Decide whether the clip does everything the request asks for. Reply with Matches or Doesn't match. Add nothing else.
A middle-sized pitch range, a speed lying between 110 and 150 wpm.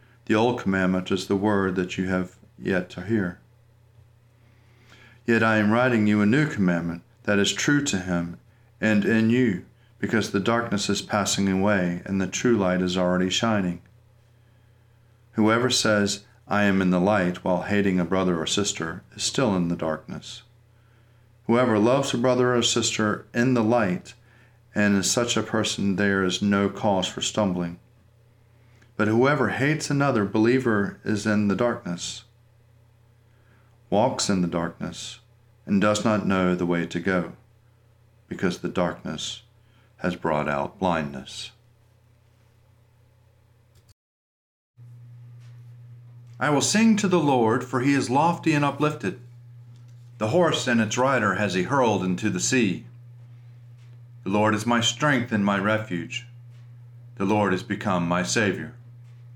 Matches